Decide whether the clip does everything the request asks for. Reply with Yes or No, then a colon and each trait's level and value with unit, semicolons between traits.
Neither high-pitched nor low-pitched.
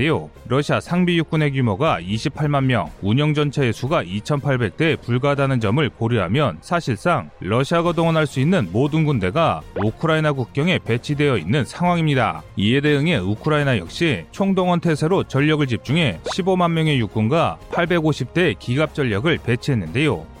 Yes: medium, 145 Hz